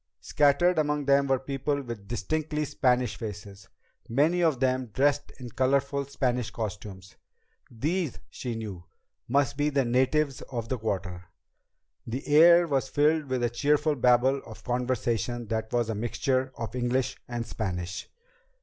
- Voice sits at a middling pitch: No, low, 130 Hz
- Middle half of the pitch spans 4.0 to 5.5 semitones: No, average, 3.6 semitones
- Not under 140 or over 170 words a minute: Yes, average, 145 wpm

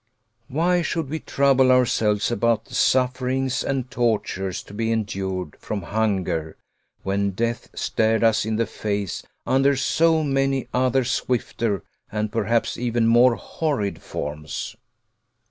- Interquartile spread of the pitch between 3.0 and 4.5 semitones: Yes, average, 4.1 semitones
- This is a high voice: No, low, 115 Hz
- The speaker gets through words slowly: Yes, slow, 130 wpm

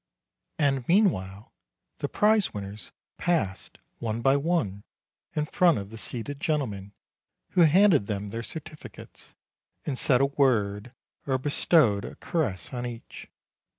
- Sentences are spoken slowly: Yes, slow, 130 wpm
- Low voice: Yes, low, 130 Hz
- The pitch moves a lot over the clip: Yes, wide, 7.1 semitones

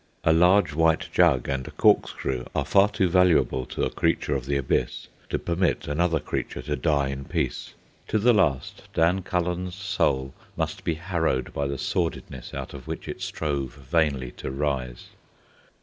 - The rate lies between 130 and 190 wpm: Yes, average, 170 wpm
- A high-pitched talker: No, very low, 75 Hz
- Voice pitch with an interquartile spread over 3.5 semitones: Yes, average, 4.7 semitones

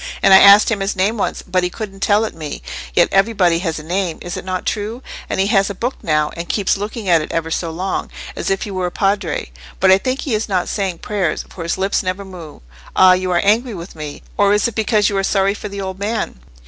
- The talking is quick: Yes, fast, 250 wpm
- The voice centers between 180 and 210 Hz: Yes, high, 195 Hz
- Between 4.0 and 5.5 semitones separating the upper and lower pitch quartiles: No, average, 2.8 semitones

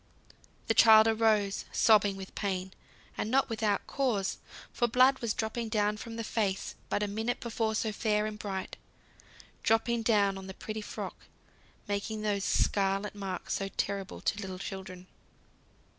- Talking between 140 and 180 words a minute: Yes, average, 155 wpm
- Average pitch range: No, narrow, 2.3 semitones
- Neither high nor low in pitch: No, high, 210 Hz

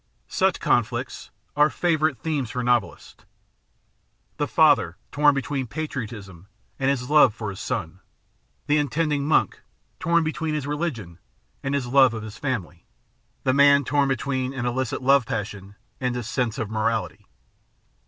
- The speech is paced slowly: No, average, 145 wpm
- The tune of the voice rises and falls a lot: No, average, 4.7 semitones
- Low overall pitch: Yes, low, 130 Hz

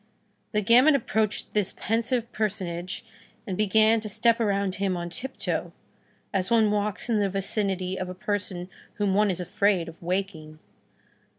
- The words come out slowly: No, average, 155 wpm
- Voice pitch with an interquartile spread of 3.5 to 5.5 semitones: No, average, 2.9 semitones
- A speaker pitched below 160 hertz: No, high, 200 Hz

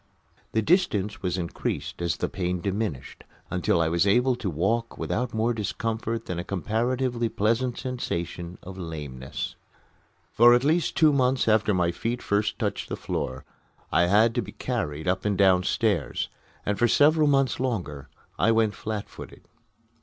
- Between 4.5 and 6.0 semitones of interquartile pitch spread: Yes, average, 5.1 semitones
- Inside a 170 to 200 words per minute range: No, average, 160 wpm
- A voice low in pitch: Yes, low, 105 Hz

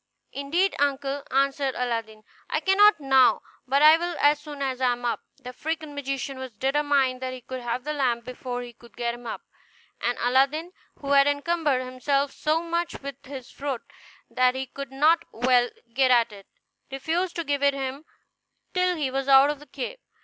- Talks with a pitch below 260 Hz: No, very high, 275 Hz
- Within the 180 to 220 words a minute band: Yes, average, 190 wpm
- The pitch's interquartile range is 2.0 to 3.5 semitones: Yes, average, 2.7 semitones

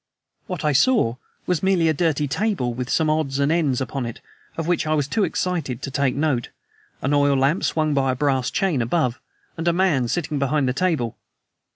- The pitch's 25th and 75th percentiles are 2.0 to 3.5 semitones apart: No, average, 4.0 semitones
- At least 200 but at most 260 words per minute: Yes, fast, 205 wpm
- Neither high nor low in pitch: Yes, medium, 145 Hz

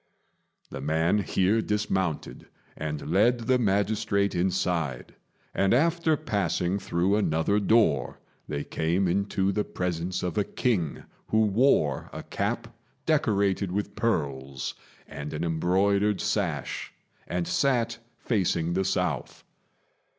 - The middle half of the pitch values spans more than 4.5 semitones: No, average, 4.1 semitones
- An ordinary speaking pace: No, slow, 115 wpm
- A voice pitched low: Yes, very low, 95 Hz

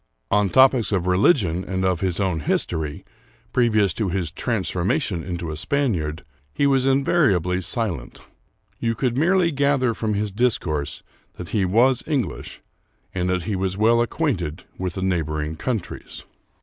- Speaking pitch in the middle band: No, very low, 95 Hz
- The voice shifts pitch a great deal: Yes, wide, 6.0 semitones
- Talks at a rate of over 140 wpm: Yes, average, 150 wpm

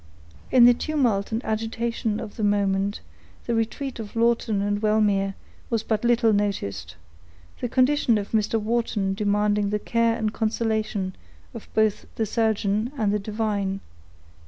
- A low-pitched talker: No, high, 215 Hz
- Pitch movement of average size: No, narrow, 2.1 semitones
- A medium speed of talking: Yes, average, 145 wpm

